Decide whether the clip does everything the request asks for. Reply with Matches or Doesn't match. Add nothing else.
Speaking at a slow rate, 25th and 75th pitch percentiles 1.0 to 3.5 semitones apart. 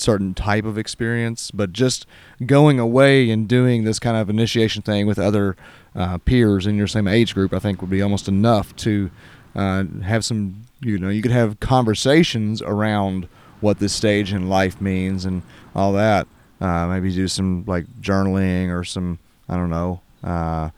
Doesn't match